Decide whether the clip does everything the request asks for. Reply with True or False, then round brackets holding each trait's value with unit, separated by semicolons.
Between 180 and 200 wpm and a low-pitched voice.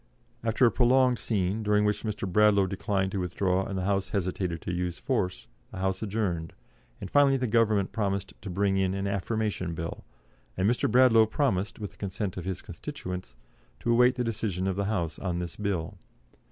True (190 wpm; 100 Hz)